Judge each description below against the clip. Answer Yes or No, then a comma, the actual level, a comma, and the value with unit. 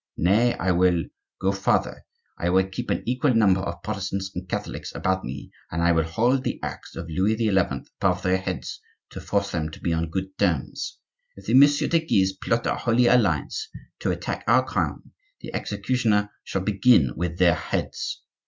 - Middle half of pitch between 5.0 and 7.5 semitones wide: No, average, 4.2 semitones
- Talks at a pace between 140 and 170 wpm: No, average, 185 wpm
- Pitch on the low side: Yes, very low, 95 Hz